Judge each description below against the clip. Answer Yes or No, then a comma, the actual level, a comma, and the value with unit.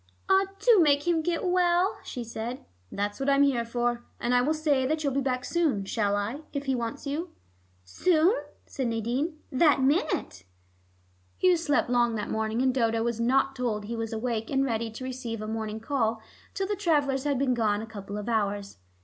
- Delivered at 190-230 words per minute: Yes, average, 200 wpm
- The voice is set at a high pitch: Yes, very high, 255 Hz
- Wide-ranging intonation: No, average, 4.5 semitones